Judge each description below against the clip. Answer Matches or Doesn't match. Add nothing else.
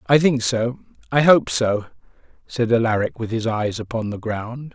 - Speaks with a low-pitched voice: Matches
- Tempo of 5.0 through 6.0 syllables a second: Doesn't match